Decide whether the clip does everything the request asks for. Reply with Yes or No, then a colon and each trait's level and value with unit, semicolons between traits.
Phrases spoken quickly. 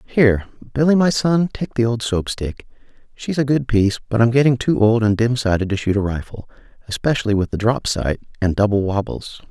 Yes: fast, 210 wpm